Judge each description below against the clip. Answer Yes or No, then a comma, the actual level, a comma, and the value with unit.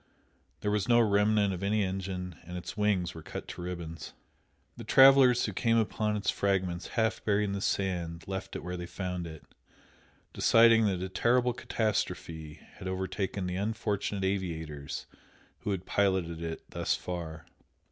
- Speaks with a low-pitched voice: Yes, very low, 95 Hz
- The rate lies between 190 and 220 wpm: No, average, 160 wpm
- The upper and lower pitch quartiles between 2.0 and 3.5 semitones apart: Yes, average, 3.1 semitones